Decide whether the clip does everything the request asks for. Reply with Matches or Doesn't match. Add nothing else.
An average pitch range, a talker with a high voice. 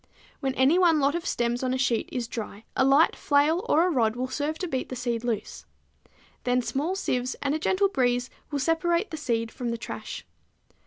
Matches